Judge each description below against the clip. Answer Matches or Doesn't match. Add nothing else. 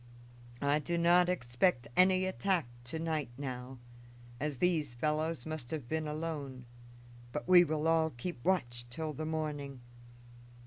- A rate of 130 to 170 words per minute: Matches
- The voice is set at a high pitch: Doesn't match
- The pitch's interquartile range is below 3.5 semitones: Doesn't match